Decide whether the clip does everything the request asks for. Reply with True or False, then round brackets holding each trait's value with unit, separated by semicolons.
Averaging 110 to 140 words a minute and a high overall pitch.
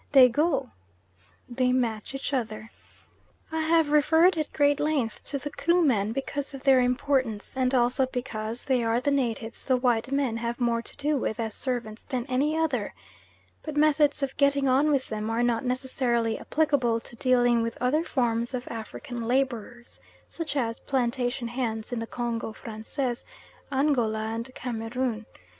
False (160 wpm; 250 Hz)